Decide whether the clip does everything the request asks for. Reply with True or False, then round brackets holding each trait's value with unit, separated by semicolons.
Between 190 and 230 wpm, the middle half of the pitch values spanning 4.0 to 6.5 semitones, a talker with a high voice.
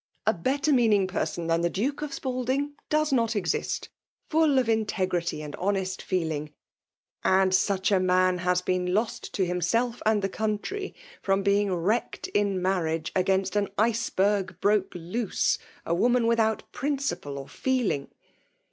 False (155 wpm; 4.4 semitones; 195 Hz)